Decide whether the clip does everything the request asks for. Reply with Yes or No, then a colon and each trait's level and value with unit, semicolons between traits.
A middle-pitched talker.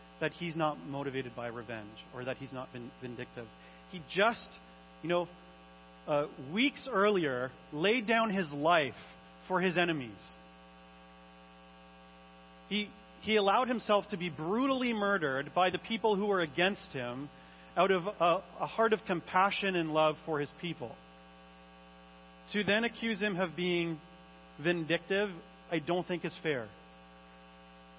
Yes: medium, 145 Hz